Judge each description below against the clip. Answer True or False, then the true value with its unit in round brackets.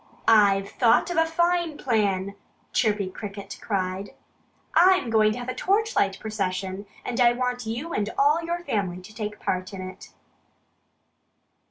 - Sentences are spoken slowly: False (150 wpm)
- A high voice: True (220 Hz)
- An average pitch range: False (6.4 semitones)